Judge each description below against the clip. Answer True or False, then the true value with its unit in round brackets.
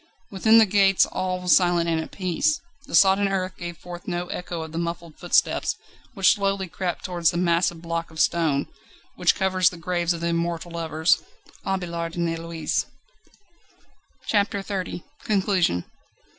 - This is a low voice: False (175 Hz)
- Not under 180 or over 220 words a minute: False (155 wpm)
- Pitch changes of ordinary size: False (2.2 semitones)